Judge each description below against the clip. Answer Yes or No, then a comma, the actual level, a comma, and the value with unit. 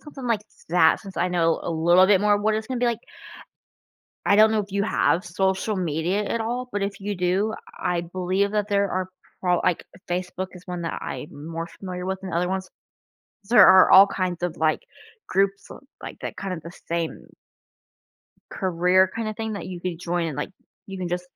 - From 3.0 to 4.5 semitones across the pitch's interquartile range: No, narrow, 2.5 semitones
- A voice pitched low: No, medium, 185 Hz